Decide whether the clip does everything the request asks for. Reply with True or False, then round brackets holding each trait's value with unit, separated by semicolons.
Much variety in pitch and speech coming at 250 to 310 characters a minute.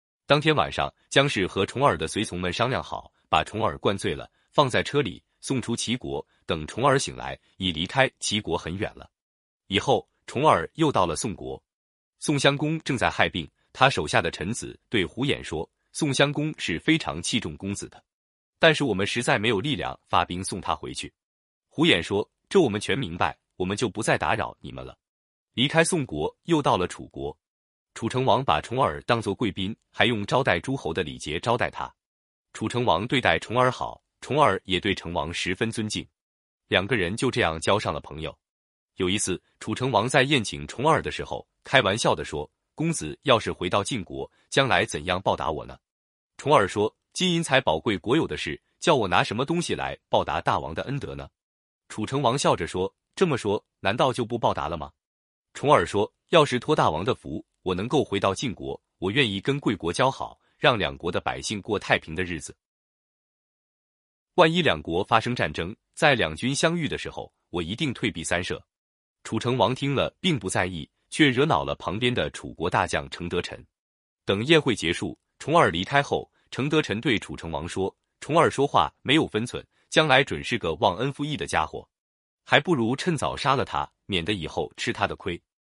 True (7.9 semitones; 275 characters per minute)